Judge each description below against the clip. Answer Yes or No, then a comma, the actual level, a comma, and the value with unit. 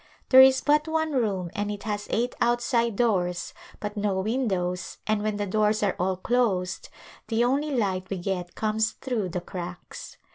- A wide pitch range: No, average, 4.3 semitones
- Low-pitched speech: No, high, 210 Hz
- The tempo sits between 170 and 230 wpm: Yes, average, 175 wpm